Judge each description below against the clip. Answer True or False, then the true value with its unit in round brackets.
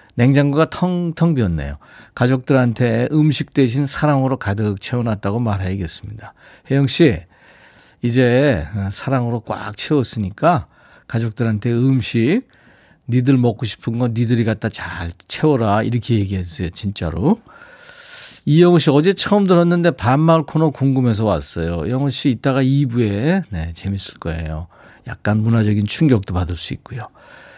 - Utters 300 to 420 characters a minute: True (305 characters per minute)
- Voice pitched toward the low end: True (120 Hz)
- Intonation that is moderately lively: False (5.8 semitones)